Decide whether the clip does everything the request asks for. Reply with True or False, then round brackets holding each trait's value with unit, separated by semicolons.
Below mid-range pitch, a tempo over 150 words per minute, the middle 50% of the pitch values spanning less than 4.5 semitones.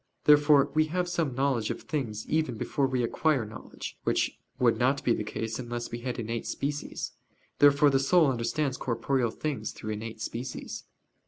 True (130 Hz; 170 wpm; 3.8 semitones)